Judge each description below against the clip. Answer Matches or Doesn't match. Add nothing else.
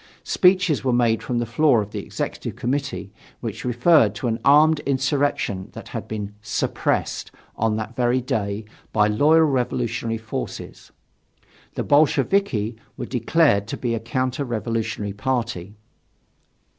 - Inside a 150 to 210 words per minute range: Doesn't match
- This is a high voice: Doesn't match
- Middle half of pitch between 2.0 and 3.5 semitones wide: Doesn't match